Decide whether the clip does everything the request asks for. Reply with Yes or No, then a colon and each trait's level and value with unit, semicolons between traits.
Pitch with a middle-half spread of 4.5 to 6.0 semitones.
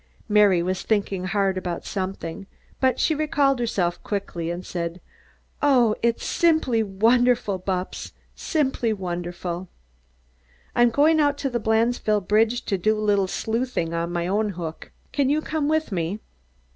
Yes: average, 5.1 semitones